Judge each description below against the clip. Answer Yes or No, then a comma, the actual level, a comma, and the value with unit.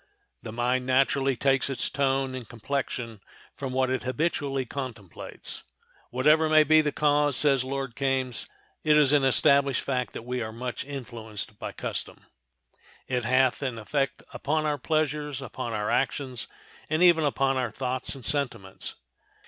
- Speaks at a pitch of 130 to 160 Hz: Yes, low, 135 Hz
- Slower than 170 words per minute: Yes, average, 155 wpm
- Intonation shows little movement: Yes, narrow, 2.3 semitones